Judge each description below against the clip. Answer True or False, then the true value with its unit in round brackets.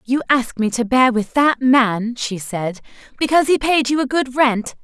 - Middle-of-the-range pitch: False (250 Hz)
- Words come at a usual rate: False (210 wpm)